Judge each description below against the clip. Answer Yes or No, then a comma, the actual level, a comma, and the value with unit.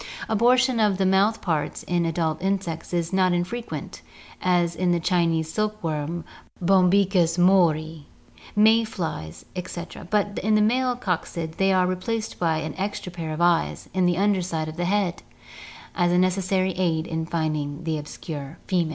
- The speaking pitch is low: No, medium, 180 Hz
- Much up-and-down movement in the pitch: No, average, 3.0 semitones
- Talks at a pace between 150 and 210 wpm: Yes, average, 165 wpm